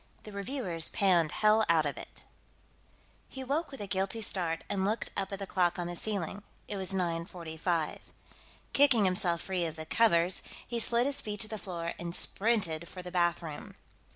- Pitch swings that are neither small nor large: Yes, average, 3.9 semitones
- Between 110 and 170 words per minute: No, average, 180 wpm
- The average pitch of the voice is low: No, high, 190 Hz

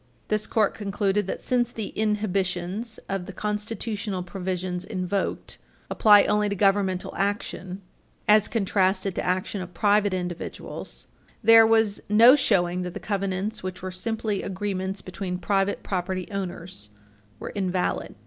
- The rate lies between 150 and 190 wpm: No, slow, 135 wpm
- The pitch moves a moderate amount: No, narrow, 2.3 semitones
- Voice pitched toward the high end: Yes, high, 195 Hz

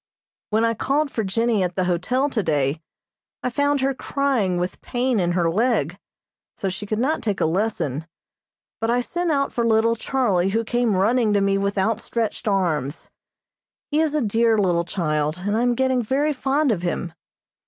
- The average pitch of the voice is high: Yes, high, 220 Hz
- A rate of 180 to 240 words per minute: Yes, average, 185 wpm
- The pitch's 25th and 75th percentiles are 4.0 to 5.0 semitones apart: No, wide, 5.5 semitones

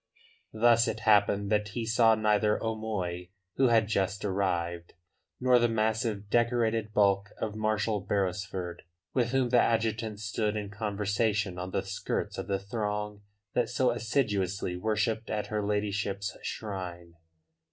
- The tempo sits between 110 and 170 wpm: Yes, average, 140 wpm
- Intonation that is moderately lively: No, narrow, 2.1 semitones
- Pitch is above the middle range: No, low, 105 Hz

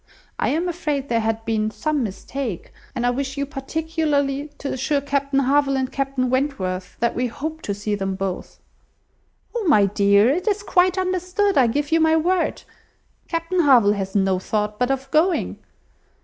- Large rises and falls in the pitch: Yes, wide, 6.3 semitones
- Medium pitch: No, very high, 275 Hz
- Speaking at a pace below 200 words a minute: Yes, average, 175 wpm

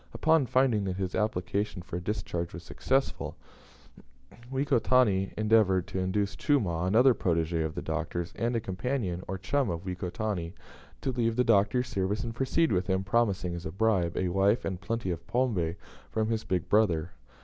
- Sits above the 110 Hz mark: No, low, 100 Hz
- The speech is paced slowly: No, average, 170 wpm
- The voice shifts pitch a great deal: No, average, 4.3 semitones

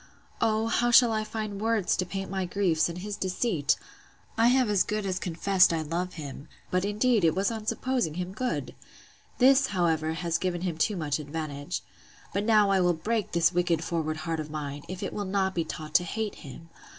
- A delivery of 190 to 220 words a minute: Yes, average, 200 wpm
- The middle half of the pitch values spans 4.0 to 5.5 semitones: Yes, average, 4.5 semitones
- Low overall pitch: No, medium, 185 Hz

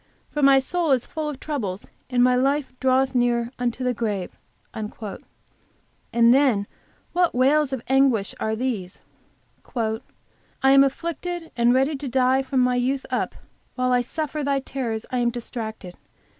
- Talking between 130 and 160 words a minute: Yes, average, 155 wpm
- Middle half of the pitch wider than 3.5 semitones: No, narrow, 2.6 semitones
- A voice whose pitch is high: Yes, very high, 255 Hz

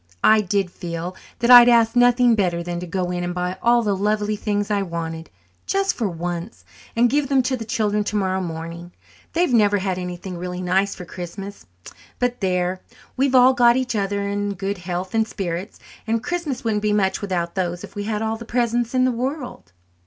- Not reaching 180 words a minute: No, fast, 205 wpm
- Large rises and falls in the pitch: No, average, 4.7 semitones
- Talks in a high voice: Yes, high, 205 Hz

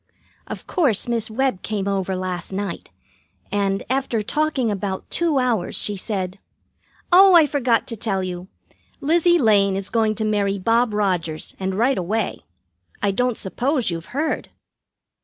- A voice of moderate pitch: No, high, 215 Hz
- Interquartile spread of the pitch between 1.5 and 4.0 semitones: No, average, 4.7 semitones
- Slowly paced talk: No, average, 150 wpm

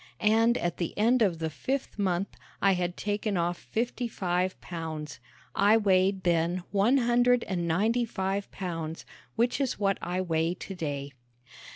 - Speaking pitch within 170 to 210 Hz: Yes, high, 190 Hz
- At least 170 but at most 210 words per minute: No, average, 155 wpm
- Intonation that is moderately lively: Yes, average, 4.3 semitones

